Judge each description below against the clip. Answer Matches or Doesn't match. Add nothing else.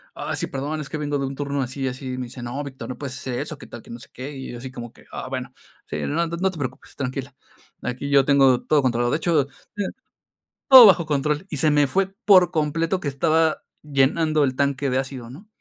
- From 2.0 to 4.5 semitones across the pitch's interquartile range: Matches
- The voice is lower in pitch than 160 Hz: Matches